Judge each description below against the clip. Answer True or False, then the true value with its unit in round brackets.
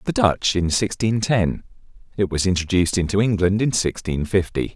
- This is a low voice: True (95 Hz)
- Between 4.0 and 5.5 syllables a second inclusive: True (5.1 syllables/s)